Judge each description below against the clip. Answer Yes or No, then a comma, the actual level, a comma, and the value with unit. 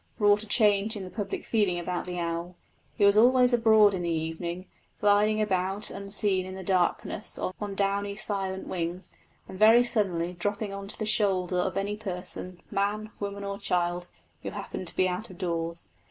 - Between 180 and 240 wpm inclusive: Yes, average, 185 wpm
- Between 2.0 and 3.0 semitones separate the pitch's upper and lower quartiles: Yes, narrow, 2.5 semitones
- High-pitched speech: Yes, high, 195 Hz